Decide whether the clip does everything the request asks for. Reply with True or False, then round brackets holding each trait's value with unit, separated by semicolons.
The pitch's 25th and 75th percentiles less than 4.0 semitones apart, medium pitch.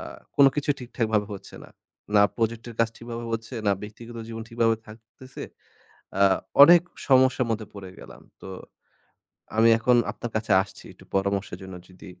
False (2.6 semitones; 115 Hz)